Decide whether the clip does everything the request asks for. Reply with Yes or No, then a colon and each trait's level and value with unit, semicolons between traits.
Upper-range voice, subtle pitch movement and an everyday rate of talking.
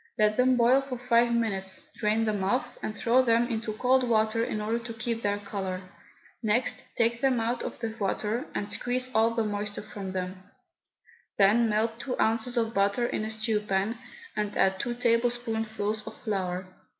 Yes: high, 225 Hz; narrow, 2.3 semitones; average, 180 wpm